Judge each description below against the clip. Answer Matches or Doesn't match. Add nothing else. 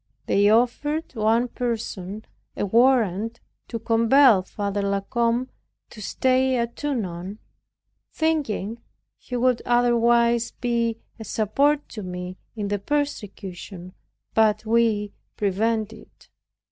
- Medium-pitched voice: Doesn't match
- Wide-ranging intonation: Doesn't match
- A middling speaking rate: Doesn't match